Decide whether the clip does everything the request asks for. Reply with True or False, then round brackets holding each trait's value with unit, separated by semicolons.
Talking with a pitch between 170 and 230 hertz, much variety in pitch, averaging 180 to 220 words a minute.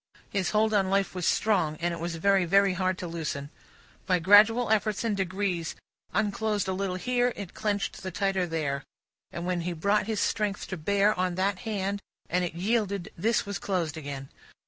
False (190 Hz; 2.9 semitones; 190 wpm)